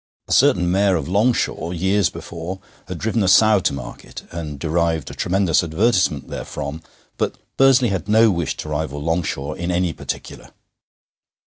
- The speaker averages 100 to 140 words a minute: No, average, 155 wpm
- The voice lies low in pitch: Yes, very low, 90 Hz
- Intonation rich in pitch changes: No, average, 3.8 semitones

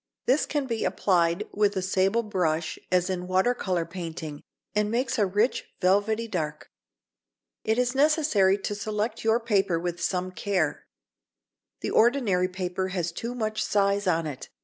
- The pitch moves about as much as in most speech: Yes, average, 3.6 semitones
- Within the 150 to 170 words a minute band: Yes, average, 155 wpm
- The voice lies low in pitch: No, high, 195 Hz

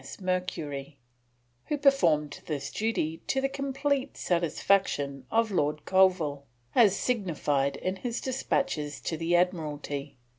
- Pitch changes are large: Yes, wide, 7.6 semitones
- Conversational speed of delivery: No, slow, 120 wpm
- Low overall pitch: No, medium, 175 Hz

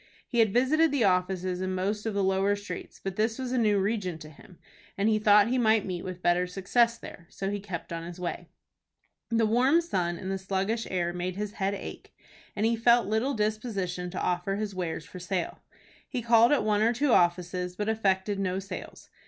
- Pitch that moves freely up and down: No, average, 3.5 semitones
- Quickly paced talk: Yes, fast, 210 wpm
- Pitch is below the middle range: No, high, 200 Hz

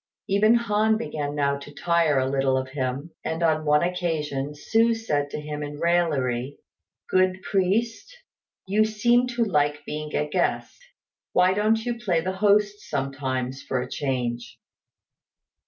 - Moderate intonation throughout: No, wide, 6.7 semitones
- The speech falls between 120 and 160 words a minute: Yes, average, 150 wpm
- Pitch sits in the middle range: Yes, medium, 160 Hz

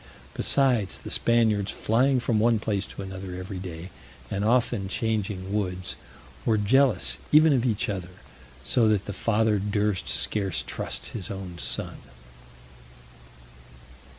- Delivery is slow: Yes, slow, 130 wpm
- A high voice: No, low, 105 Hz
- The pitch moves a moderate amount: Yes, average, 3.2 semitones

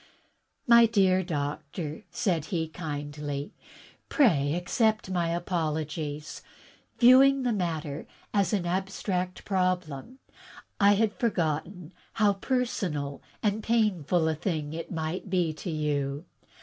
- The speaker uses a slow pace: Yes, slow, 110 wpm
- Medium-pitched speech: Yes, medium, 175 Hz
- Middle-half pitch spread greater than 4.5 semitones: Yes, average, 4.9 semitones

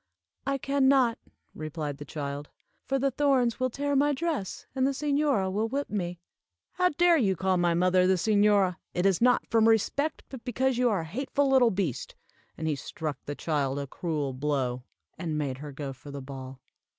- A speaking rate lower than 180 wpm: No, average, 195 wpm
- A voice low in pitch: No, high, 195 Hz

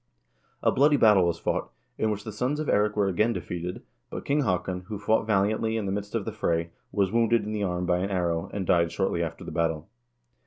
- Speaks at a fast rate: Yes, fast, 230 wpm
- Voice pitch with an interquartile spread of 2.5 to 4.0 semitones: Yes, average, 3.6 semitones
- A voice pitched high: No, low, 100 Hz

